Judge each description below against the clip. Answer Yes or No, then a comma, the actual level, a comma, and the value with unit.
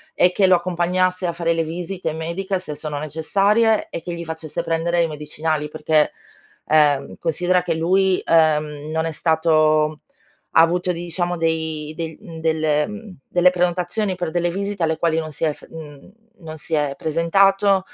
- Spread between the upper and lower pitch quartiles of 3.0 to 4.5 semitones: No, narrow, 2.4 semitones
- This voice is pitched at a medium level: Yes, medium, 165 Hz